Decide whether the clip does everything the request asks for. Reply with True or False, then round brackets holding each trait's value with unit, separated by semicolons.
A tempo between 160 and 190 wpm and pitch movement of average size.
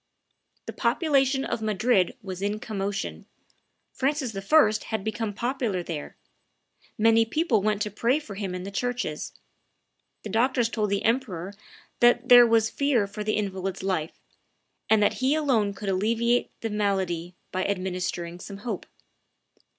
False (145 wpm; 3.8 semitones)